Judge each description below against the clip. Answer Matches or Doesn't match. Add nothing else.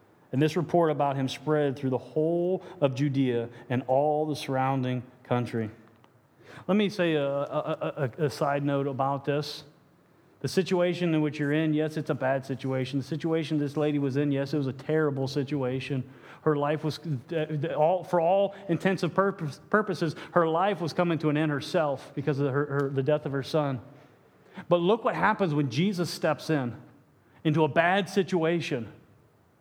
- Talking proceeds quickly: Doesn't match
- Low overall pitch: Doesn't match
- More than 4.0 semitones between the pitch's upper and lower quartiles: Doesn't match